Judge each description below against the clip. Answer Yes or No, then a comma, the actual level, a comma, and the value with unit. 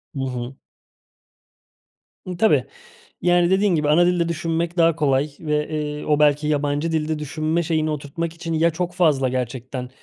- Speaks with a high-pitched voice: No, medium, 155 Hz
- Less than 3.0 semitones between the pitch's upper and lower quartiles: Yes, narrow, 2.5 semitones